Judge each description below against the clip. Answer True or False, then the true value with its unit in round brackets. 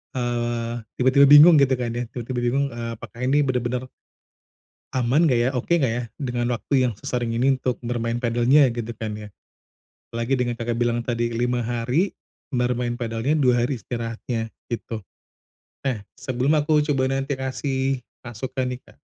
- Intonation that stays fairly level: True (2.0 semitones)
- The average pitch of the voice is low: True (125 Hz)